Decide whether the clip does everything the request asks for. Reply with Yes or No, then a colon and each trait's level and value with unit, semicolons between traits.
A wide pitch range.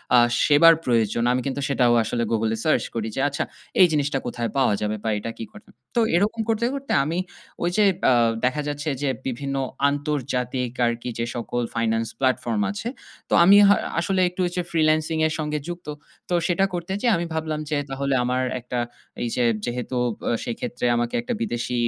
Yes: wide, 5.7 semitones